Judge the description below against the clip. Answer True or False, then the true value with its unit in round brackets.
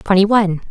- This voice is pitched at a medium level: False (195 Hz)